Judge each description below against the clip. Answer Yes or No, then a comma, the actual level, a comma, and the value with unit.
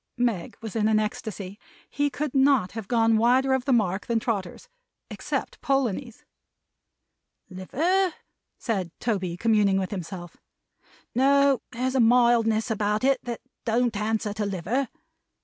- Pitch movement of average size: Yes, average, 4.1 semitones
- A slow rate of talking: Yes, slow, 130 wpm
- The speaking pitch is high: Yes, high, 225 Hz